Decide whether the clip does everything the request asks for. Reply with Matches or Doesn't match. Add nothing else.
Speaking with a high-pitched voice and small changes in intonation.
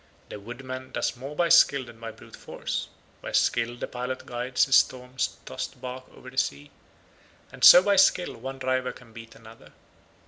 Doesn't match